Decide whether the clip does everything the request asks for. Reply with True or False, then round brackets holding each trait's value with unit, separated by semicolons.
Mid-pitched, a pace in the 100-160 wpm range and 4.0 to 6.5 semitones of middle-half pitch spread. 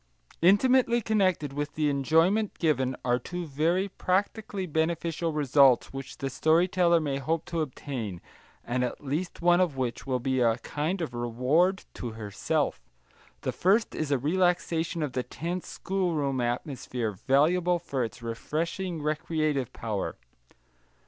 True (155 Hz; 140 wpm; 5.2 semitones)